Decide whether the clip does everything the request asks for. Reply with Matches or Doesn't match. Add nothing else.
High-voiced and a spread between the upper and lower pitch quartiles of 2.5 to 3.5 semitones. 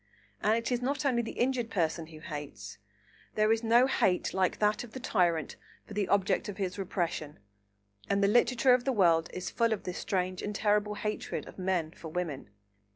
Doesn't match